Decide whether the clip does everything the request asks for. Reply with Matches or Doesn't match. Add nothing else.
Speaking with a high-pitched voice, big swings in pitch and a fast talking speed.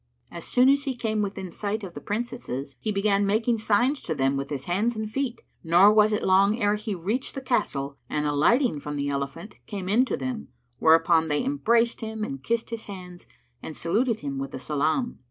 Matches